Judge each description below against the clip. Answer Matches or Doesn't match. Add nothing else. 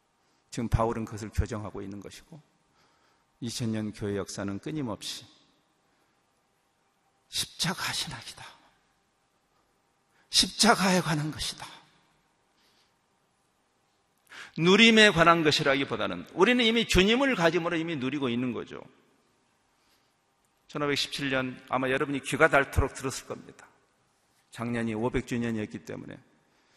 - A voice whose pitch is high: Doesn't match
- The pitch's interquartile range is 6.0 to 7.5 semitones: Doesn't match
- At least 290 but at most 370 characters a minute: Doesn't match